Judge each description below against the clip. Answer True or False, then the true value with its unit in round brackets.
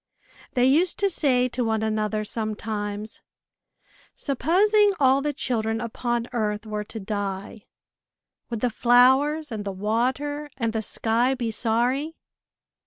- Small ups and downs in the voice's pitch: False (3.7 semitones)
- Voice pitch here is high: True (235 Hz)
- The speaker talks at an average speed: False (130 wpm)